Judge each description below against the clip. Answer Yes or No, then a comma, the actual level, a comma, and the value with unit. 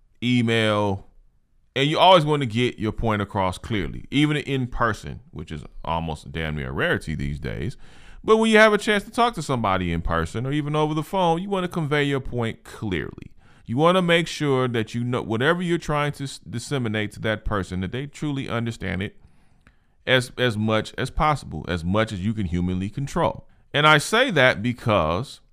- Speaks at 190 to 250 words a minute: Yes, average, 200 wpm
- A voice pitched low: Yes, low, 120 Hz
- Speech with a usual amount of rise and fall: No, wide, 6.4 semitones